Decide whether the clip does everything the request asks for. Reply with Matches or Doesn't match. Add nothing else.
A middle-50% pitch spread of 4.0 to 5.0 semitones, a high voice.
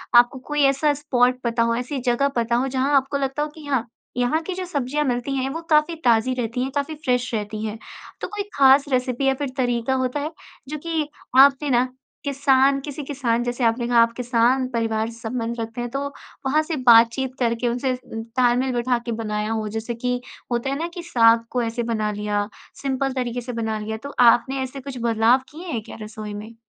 Doesn't match